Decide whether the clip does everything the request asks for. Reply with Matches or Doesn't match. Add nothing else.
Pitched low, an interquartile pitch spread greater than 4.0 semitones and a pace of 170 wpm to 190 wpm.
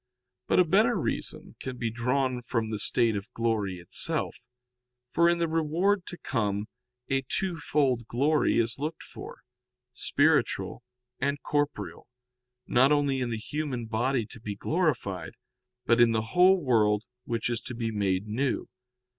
Doesn't match